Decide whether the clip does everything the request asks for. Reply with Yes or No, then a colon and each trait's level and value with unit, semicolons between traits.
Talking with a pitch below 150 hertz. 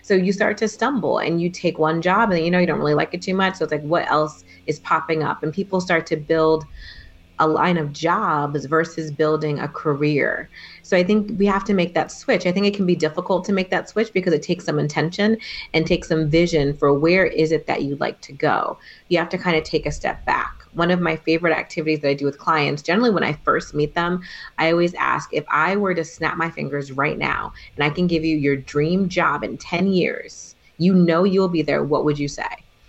No: medium, 165 Hz